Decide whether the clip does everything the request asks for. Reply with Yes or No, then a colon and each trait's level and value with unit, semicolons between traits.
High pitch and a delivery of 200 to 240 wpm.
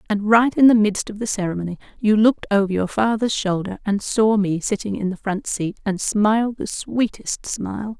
Yes: high, 210 Hz; fast, 205 wpm